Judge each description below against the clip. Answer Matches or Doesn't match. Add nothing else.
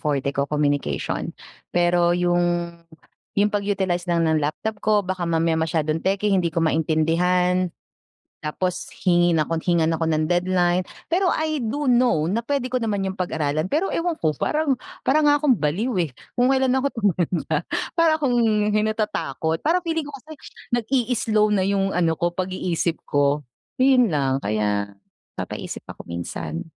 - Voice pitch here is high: Doesn't match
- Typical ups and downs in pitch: Doesn't match